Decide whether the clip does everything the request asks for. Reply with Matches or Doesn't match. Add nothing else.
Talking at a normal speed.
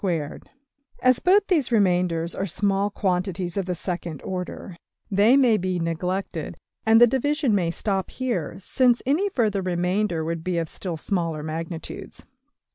Matches